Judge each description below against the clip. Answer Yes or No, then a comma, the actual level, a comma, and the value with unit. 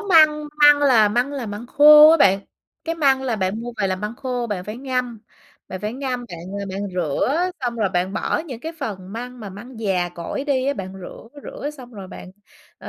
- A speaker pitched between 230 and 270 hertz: Yes, high, 240 Hz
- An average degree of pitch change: No, wide, 5.9 semitones